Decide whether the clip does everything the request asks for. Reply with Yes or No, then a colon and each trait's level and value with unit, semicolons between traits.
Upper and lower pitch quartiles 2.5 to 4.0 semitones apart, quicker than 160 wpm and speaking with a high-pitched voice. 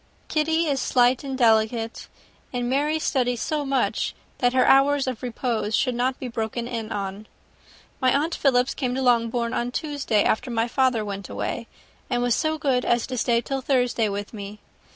Yes: average, 2.8 semitones; average, 180 wpm; high, 245 Hz